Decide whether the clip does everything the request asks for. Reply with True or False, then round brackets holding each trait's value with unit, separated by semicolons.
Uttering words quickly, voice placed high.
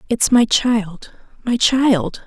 False (130 wpm; 225 Hz)